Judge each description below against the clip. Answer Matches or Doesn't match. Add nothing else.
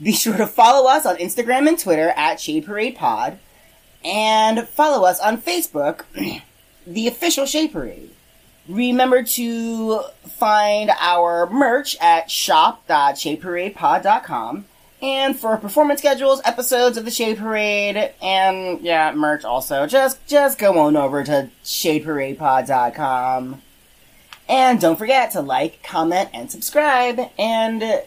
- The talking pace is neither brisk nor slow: Doesn't match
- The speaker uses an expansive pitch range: Matches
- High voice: Matches